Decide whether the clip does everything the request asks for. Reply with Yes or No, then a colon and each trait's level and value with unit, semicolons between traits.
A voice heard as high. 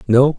No: low, 130 Hz